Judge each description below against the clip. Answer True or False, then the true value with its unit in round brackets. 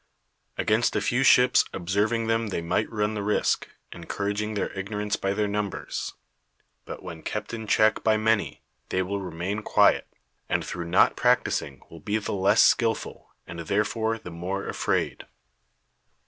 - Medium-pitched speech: False (105 Hz)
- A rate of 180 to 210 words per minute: False (155 wpm)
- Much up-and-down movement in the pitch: False (2.6 semitones)